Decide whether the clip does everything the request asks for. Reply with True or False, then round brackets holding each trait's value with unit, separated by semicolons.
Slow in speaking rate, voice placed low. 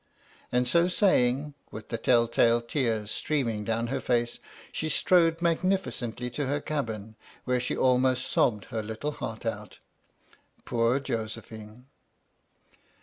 True (130 wpm; 120 Hz)